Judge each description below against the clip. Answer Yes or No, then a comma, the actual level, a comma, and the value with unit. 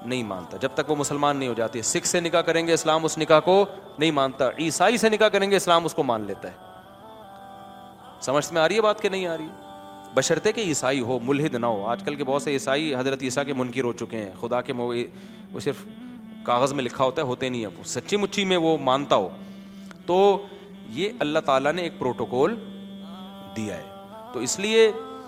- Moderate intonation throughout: No, wide, 6.9 semitones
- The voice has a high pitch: No, medium, 160 Hz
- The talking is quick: Yes, fast, 205 wpm